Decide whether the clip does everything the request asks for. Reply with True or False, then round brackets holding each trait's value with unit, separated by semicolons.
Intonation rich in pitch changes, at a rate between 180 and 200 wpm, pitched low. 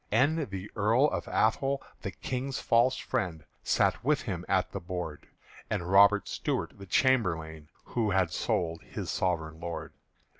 False (5.8 semitones; 150 wpm; 95 Hz)